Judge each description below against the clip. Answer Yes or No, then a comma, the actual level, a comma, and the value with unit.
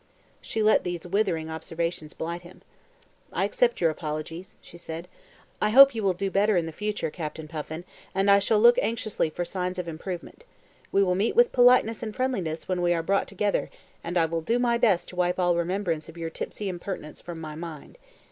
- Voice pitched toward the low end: No, medium, 180 Hz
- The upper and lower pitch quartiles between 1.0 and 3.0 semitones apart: No, average, 4.0 semitones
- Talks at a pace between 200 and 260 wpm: Yes, fast, 205 wpm